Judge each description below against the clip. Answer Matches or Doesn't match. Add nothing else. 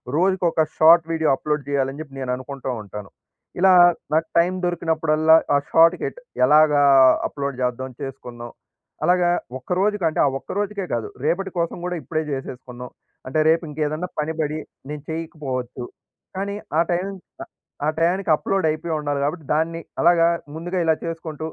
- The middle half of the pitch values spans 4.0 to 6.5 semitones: Doesn't match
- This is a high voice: Doesn't match